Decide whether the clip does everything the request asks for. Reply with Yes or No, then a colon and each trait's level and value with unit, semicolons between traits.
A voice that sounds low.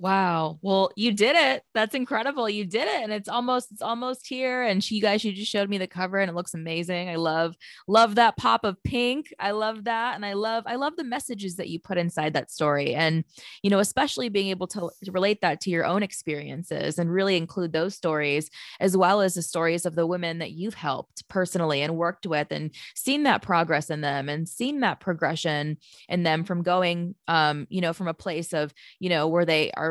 No: medium, 185 Hz